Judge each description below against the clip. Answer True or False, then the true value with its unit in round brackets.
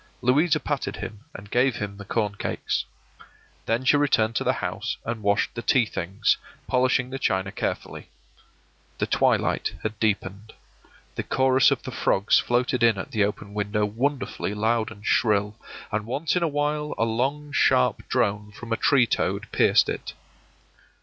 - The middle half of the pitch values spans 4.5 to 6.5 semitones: False (4.1 semitones)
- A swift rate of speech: False (165 wpm)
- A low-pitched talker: True (115 Hz)